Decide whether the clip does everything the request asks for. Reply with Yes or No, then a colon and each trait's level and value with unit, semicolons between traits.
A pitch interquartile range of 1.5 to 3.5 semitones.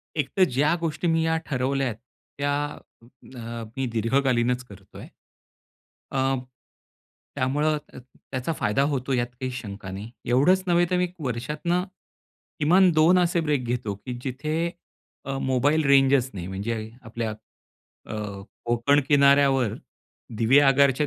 No: average, 3.9 semitones